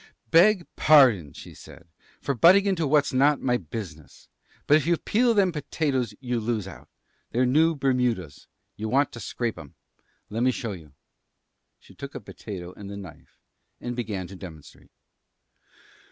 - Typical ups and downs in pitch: No, wide, 7.1 semitones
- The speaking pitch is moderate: No, low, 120 Hz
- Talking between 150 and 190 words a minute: Yes, average, 155 wpm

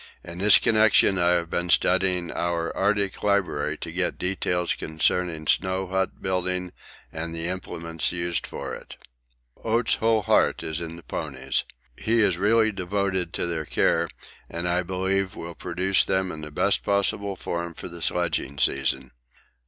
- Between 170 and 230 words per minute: No, average, 160 wpm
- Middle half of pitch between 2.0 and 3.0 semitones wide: Yes, narrow, 2.5 semitones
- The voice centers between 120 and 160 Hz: No, very low, 90 Hz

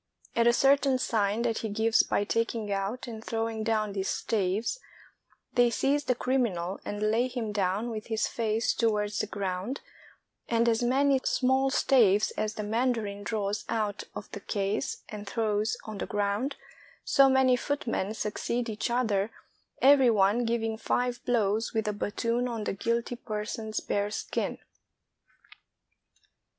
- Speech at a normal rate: Yes, average, 155 wpm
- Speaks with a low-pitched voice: No, high, 225 Hz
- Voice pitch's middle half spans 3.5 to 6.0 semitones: No, average, 2.7 semitones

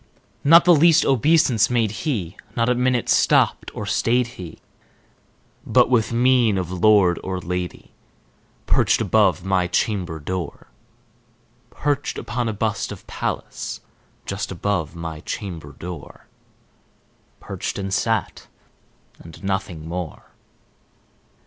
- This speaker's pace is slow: Yes, slow, 115 wpm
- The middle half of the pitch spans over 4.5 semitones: Yes, average, 5.3 semitones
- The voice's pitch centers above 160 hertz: No, low, 100 Hz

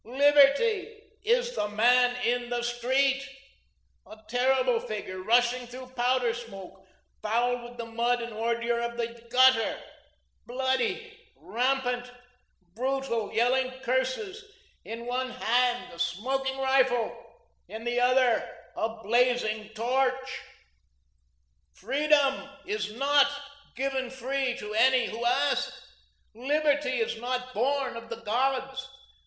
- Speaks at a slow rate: Yes, slow, 115 wpm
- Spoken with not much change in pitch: Yes, narrow, 2.2 semitones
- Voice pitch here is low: No, very high, 250 Hz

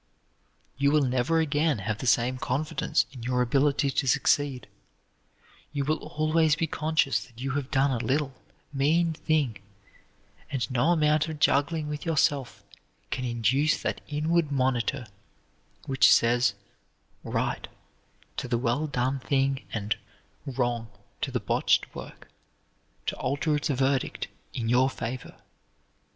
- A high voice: No, low, 135 Hz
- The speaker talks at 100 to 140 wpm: Yes, slow, 135 wpm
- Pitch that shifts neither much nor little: Yes, average, 3.3 semitones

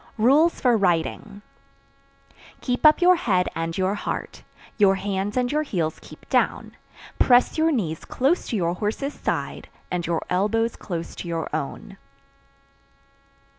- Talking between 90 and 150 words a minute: Yes, average, 140 wpm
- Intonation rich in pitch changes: Yes, wide, 6.2 semitones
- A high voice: Yes, high, 205 Hz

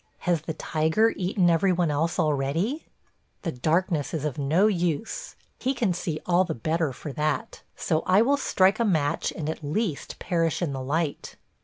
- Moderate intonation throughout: Yes, average, 3.6 semitones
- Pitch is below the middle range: No, medium, 165 Hz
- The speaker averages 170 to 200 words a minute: Yes, average, 180 wpm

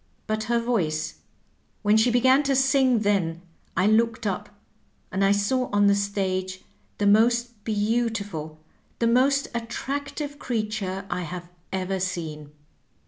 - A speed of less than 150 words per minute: Yes, average, 140 wpm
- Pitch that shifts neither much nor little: Yes, average, 4.1 semitones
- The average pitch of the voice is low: No, high, 210 Hz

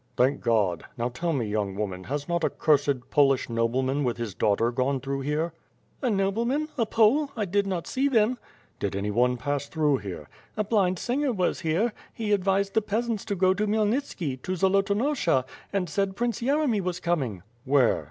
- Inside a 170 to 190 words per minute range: Yes, average, 180 wpm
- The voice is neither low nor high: Yes, medium, 175 Hz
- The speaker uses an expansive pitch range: Yes, wide, 8.6 semitones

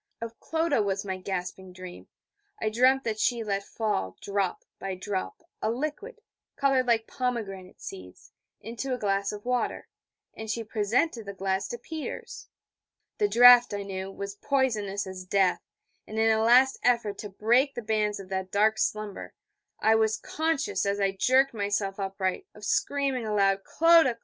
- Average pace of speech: Yes, average, 165 wpm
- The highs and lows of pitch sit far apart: No, average, 4.0 semitones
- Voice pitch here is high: Yes, high, 215 Hz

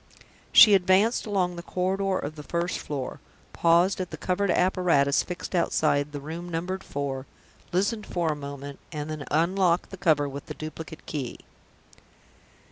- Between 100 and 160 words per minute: Yes, average, 155 wpm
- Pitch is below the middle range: No, medium, 170 Hz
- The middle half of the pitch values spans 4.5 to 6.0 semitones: No, average, 4.1 semitones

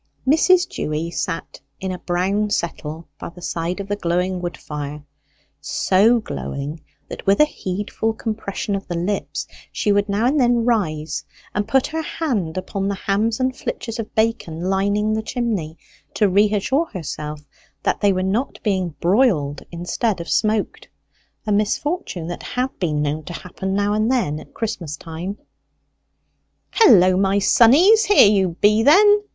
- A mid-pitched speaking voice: No, high, 200 Hz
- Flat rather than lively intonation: No, average, 4.6 semitones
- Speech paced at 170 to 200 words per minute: No, average, 160 wpm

